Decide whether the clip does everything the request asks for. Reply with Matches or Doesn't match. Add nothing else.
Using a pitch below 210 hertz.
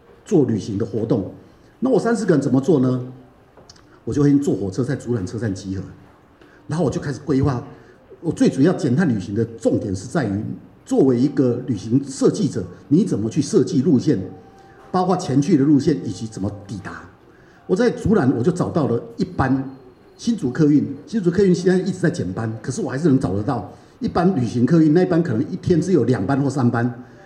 Matches